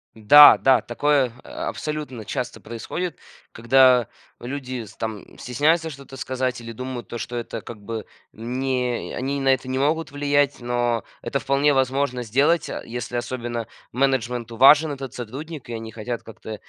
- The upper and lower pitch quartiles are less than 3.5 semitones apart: Yes, average, 2.9 semitones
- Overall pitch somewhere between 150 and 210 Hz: No, low, 130 Hz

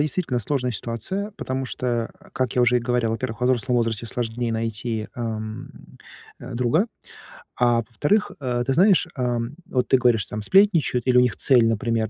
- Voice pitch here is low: Yes, low, 125 Hz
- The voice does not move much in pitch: Yes, narrow, 2.3 semitones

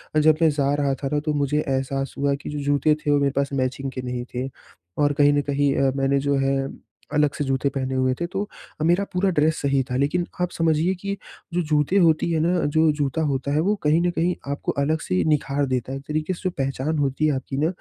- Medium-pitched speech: Yes, medium, 145 Hz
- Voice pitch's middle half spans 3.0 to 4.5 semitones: No, narrow, 2.6 semitones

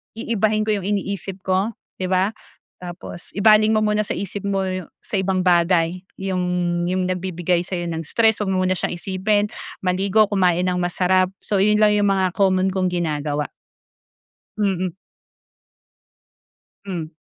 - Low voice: No, medium, 185 Hz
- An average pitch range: No, narrow, 2.1 semitones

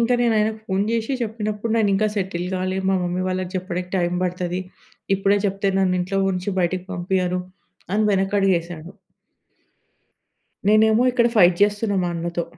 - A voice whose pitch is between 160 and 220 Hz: Yes, high, 190 Hz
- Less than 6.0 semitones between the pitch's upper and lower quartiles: Yes, average, 2.7 semitones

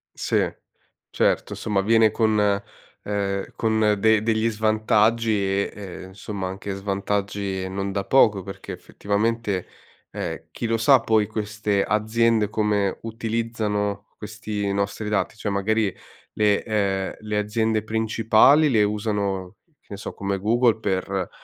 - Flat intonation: Yes, narrow, 1.9 semitones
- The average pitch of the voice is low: Yes, low, 105 Hz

